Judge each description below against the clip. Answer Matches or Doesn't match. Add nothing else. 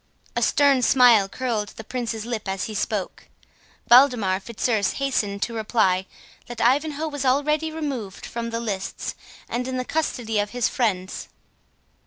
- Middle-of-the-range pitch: Doesn't match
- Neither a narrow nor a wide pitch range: Matches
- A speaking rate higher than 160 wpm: Doesn't match